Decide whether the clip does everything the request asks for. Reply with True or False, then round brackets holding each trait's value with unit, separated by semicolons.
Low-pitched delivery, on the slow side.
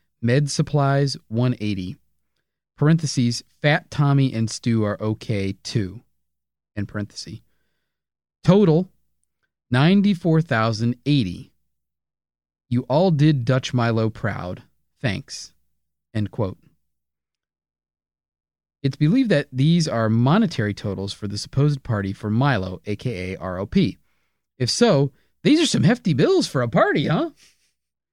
True (115 Hz; 105 wpm)